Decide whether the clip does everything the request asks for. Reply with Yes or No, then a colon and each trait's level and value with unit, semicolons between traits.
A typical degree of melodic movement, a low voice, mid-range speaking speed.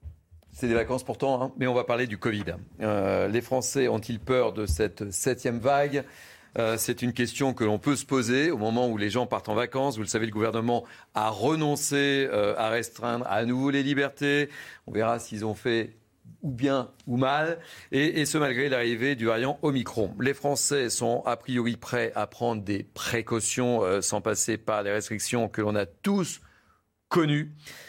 Yes: average, 4.0 semitones; low, 120 Hz; average, 190 wpm